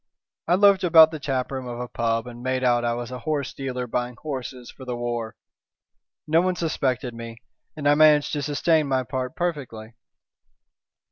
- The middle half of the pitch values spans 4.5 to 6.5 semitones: No, average, 3.9 semitones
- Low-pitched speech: Yes, low, 130 Hz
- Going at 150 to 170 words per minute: No, average, 180 wpm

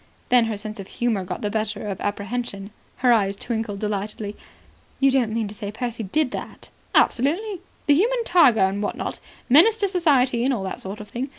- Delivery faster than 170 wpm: Yes, average, 200 wpm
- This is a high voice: Yes, high, 225 Hz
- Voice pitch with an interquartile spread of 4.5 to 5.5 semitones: Yes, average, 4.8 semitones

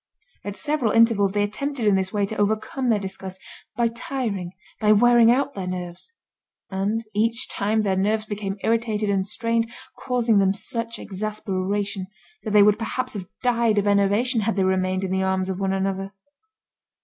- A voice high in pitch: Yes, high, 210 Hz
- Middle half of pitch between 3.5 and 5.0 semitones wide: No, average, 3.0 semitones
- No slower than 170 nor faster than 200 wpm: Yes, average, 175 wpm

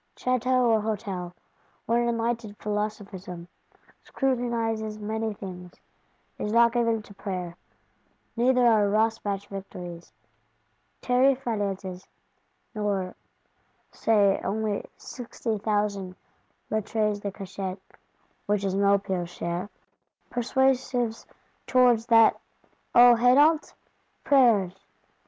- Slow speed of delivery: Yes, slow, 95 wpm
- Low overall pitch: No, high, 215 Hz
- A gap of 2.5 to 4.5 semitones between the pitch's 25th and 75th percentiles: Yes, average, 3.2 semitones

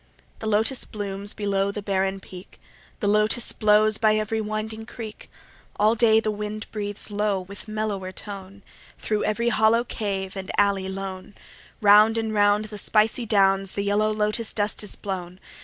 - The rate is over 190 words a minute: No, average, 165 wpm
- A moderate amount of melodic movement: No, narrow, 1.6 semitones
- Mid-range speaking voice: No, high, 210 Hz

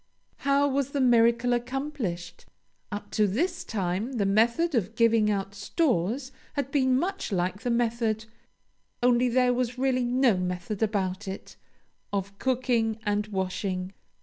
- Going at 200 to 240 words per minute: No, average, 140 wpm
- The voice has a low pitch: No, high, 230 Hz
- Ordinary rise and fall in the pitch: Yes, average, 4.3 semitones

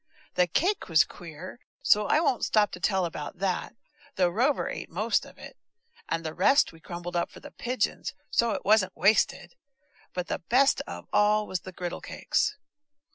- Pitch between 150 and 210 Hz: Yes, medium, 185 Hz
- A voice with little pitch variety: No, average, 4.0 semitones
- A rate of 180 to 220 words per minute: Yes, average, 185 wpm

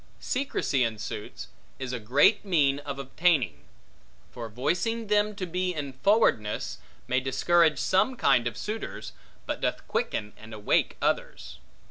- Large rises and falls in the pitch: Yes, wide, 7.8 semitones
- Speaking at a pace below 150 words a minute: Yes, average, 140 wpm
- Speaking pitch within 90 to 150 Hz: Yes, medium, 140 Hz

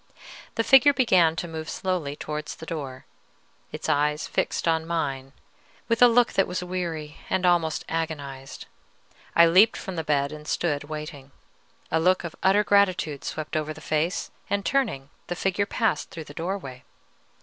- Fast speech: No, average, 165 wpm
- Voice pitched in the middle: Yes, medium, 165 Hz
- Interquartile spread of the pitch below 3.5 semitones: No, average, 3.8 semitones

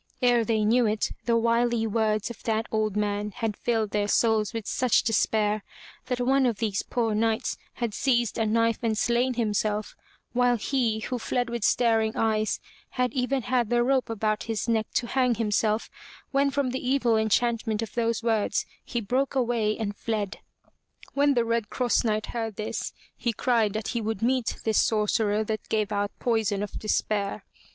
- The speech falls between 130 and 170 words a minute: No, average, 180 wpm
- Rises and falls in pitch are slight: Yes, narrow, 2.1 semitones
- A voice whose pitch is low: No, high, 225 Hz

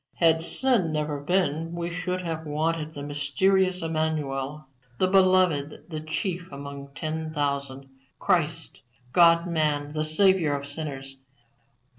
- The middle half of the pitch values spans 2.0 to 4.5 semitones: Yes, average, 3.1 semitones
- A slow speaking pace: Yes, slow, 125 wpm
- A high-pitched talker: No, medium, 155 Hz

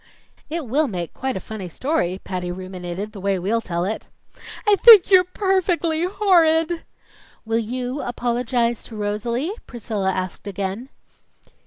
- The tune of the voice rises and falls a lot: Yes, wide, 8.7 semitones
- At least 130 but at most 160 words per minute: Yes, average, 140 wpm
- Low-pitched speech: No, high, 235 Hz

